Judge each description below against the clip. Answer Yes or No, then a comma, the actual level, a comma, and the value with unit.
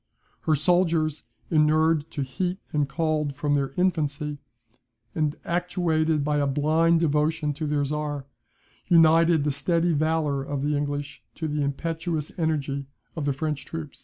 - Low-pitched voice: No, medium, 150 Hz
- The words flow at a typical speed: Yes, average, 145 wpm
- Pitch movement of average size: No, narrow, 2.2 semitones